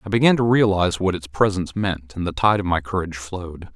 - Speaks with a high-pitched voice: No, very low, 95 Hz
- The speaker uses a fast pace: Yes, fast, 240 wpm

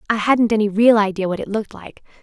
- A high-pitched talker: Yes, high, 215 Hz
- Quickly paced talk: Yes, fast, 240 wpm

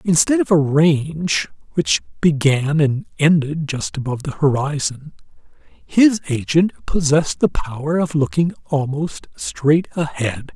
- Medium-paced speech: No, slow, 125 wpm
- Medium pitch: Yes, medium, 150 Hz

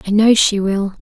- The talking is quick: Yes, fast, 235 wpm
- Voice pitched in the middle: No, high, 205 Hz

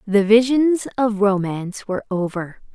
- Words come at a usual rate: No, slow, 130 wpm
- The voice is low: No, high, 210 Hz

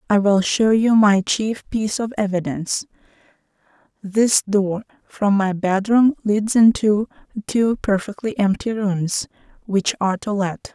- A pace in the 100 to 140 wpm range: Yes, slow, 135 wpm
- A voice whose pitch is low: No, high, 205 Hz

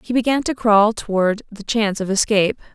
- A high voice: Yes, high, 215 Hz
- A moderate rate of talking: Yes, average, 195 wpm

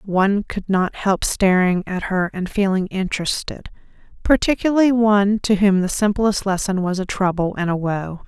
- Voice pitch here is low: No, high, 195 Hz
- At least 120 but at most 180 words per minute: Yes, average, 165 wpm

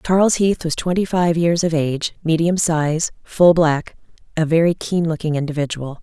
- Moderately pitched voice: Yes, medium, 165 Hz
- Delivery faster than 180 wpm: No, average, 170 wpm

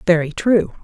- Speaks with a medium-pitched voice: Yes, medium, 180 Hz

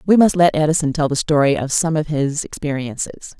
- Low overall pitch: No, medium, 150 Hz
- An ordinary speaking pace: No, fast, 210 wpm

